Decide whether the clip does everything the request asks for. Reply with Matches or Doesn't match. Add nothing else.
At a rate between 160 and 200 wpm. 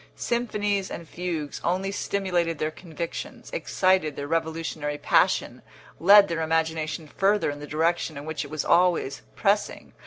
Doesn't match